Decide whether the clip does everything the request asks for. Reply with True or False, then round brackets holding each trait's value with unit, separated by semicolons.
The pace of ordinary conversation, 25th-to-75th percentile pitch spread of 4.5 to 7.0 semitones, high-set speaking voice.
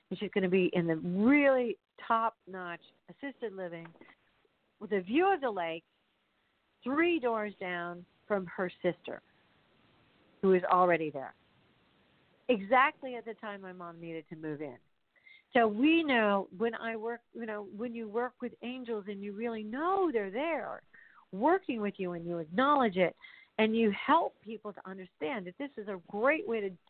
True (170 wpm; 5.2 semitones; 215 Hz)